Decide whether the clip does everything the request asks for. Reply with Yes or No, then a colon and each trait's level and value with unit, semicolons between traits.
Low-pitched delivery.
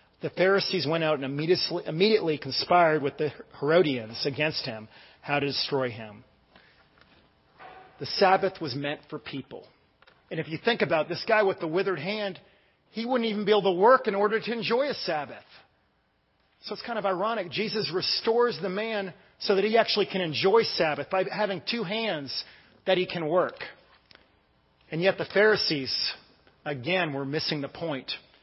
No: medium, 185 Hz